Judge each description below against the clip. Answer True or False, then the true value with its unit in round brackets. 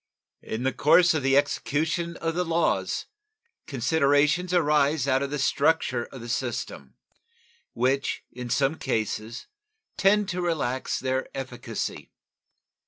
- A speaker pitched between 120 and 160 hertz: True (140 Hz)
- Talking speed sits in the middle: False (125 wpm)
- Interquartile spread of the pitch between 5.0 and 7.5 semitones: False (4.1 semitones)